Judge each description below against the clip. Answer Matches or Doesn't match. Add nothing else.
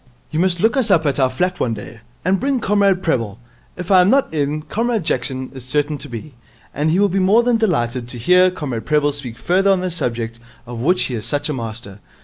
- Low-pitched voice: Doesn't match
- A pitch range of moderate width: Doesn't match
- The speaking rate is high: Matches